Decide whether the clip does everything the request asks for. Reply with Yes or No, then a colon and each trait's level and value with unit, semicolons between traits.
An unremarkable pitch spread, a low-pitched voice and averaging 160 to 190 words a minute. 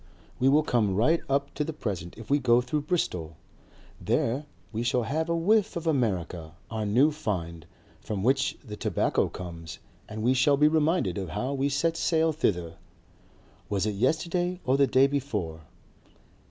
No: wide, 7.1 semitones; low, 130 Hz; average, 170 wpm